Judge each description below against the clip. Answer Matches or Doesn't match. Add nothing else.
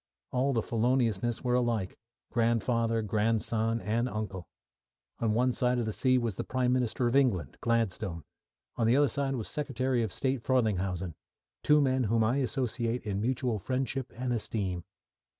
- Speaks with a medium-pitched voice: Doesn't match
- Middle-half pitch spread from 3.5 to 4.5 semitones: Doesn't match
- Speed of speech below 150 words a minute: Doesn't match